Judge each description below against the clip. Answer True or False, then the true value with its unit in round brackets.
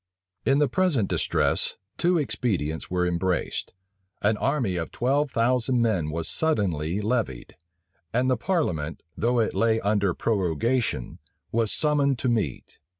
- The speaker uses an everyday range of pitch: False (6.5 semitones)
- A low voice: True (115 Hz)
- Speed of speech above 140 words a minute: False (135 wpm)